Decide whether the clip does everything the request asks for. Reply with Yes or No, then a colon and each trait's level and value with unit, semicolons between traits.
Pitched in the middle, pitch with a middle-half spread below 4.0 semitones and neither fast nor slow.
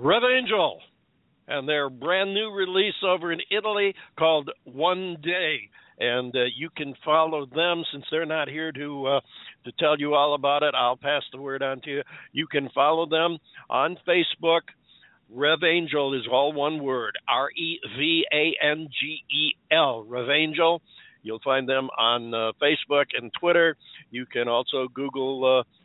Yes: medium, 150 Hz; average, 3.6 semitones; average, 165 wpm